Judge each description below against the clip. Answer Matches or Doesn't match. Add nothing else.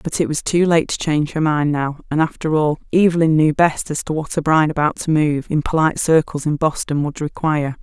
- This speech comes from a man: Doesn't match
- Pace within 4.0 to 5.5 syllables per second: Doesn't match